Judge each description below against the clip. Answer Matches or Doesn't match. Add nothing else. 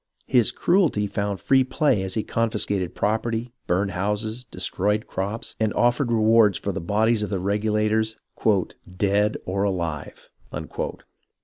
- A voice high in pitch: Doesn't match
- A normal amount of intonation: Doesn't match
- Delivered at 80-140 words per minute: Matches